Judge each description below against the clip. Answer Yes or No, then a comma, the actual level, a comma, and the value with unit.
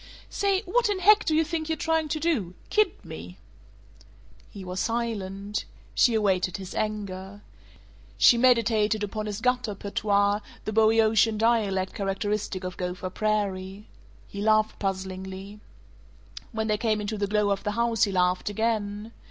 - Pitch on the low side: No, high, 210 Hz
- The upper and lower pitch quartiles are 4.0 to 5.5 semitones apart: No, average, 2.9 semitones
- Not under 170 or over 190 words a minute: No, average, 150 wpm